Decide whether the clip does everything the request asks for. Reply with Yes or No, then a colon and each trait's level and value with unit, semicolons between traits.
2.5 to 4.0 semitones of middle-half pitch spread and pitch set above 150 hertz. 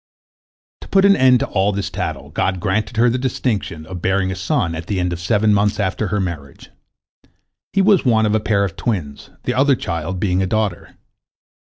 No: average, 3.5 semitones; low, 100 Hz